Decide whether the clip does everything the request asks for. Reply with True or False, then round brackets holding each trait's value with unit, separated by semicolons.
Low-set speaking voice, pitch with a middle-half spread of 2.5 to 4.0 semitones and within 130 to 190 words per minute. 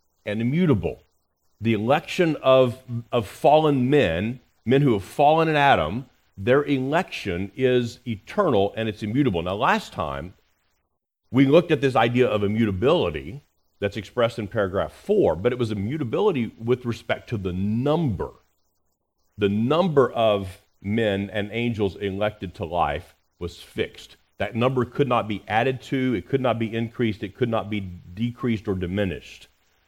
False (110 Hz; 4.7 semitones; 150 wpm)